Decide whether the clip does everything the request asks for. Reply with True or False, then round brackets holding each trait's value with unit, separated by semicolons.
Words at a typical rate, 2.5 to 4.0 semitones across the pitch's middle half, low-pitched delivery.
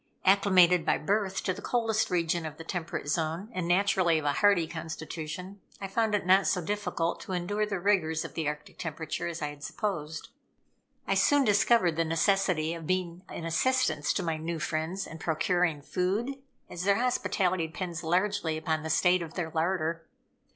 False (180 wpm; 3.4 semitones; 175 Hz)